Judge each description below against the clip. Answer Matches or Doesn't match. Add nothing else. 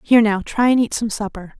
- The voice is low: Doesn't match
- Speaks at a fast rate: Matches